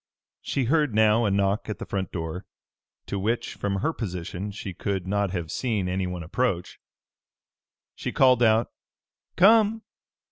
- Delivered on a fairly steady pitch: No, average, 4.4 semitones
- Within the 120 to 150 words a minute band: Yes, average, 145 wpm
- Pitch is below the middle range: Yes, low, 100 Hz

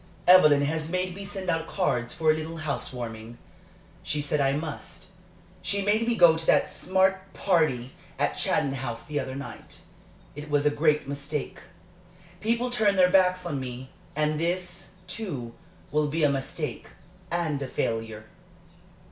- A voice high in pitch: No, medium, 155 Hz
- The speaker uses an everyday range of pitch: Yes, average, 4.7 semitones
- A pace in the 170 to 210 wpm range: No, average, 160 wpm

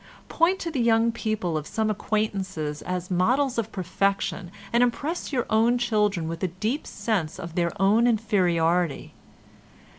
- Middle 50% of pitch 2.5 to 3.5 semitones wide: No, average, 4.8 semitones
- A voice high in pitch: Yes, high, 210 Hz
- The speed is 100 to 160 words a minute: Yes, average, 150 wpm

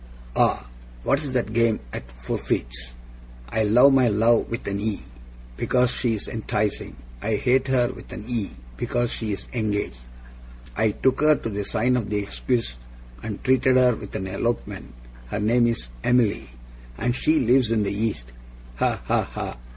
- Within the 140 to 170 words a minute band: Yes, average, 155 wpm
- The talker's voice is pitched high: No, low, 115 Hz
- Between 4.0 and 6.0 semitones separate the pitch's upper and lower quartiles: No, average, 3.4 semitones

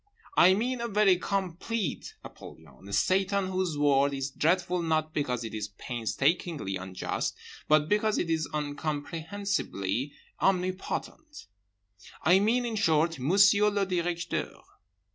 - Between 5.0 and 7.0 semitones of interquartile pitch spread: Yes, wide, 5.4 semitones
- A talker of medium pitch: Yes, medium, 170 Hz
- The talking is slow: Yes, slow, 125 wpm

